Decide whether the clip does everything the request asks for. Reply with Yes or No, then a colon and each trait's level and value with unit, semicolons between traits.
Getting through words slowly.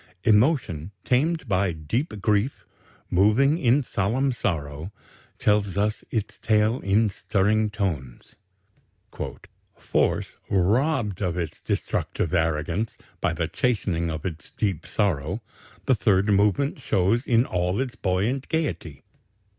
Yes: slow, 115 wpm